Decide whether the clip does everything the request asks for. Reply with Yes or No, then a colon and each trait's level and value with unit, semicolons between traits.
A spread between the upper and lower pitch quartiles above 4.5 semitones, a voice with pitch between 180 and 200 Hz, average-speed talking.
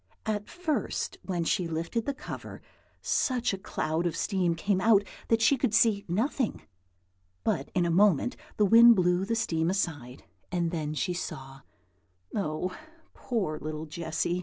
Yes: average, 5.2 semitones; medium, 185 Hz; average, 155 wpm